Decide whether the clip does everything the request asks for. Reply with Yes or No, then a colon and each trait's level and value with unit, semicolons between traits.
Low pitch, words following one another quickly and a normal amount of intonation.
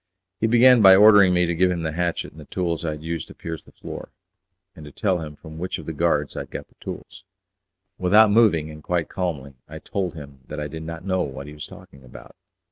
Yes: very low, 85 Hz; fast, 245 wpm; average, 3.4 semitones